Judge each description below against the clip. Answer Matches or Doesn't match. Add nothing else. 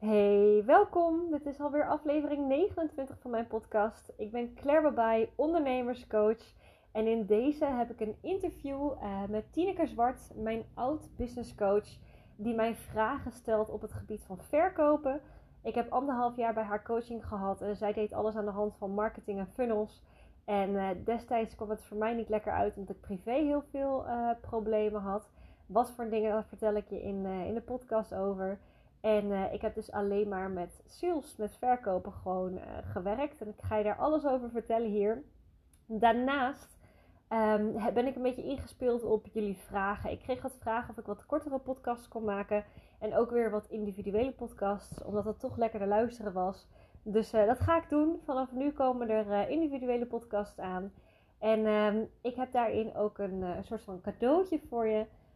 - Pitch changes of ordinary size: Matches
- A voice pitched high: Matches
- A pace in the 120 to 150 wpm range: Doesn't match